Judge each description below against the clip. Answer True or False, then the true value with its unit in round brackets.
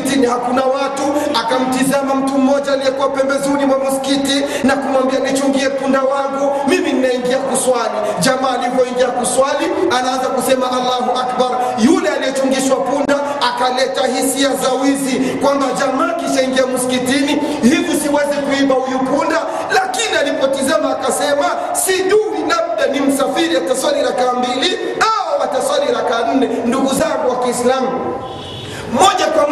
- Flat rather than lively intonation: True (1.9 semitones)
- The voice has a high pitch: True (270 Hz)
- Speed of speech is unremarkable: True (110 wpm)